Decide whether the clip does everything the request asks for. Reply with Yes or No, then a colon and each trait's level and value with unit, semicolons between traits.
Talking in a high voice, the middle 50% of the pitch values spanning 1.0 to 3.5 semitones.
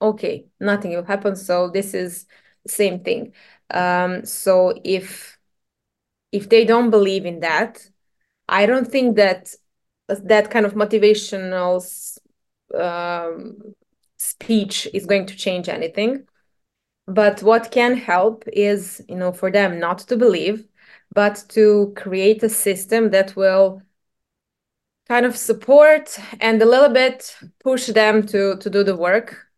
Yes: high, 205 Hz; average, 2.8 semitones